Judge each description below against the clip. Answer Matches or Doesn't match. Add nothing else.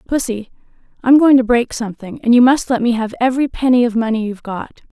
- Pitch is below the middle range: Doesn't match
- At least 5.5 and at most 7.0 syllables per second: Matches